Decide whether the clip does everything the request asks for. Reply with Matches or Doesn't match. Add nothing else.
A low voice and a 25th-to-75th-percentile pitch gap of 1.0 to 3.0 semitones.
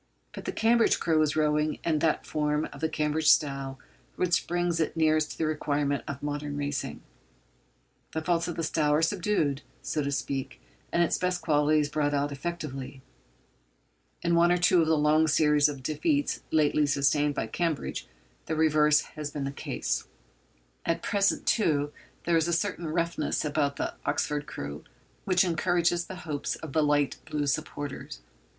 Doesn't match